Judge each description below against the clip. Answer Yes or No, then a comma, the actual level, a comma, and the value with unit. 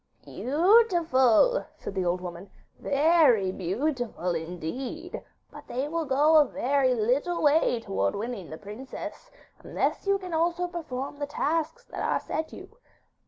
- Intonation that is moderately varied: No, wide, 7.5 semitones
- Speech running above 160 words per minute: No, average, 140 wpm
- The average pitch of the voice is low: No, very high, 275 Hz